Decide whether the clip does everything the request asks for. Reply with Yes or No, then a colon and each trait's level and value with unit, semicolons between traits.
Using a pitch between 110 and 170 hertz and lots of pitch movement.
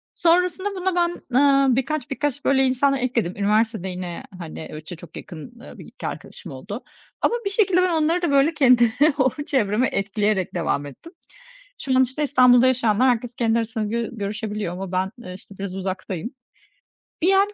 No: high, 240 Hz; wide, 6.1 semitones